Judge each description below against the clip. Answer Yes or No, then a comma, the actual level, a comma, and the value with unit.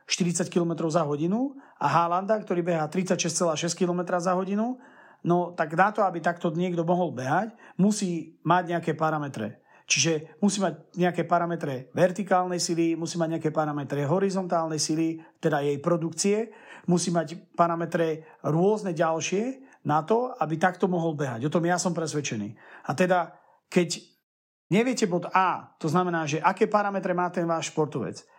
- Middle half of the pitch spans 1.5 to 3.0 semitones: Yes, narrow, 2.4 semitones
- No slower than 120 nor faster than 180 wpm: Yes, average, 150 wpm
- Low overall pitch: No, medium, 175 Hz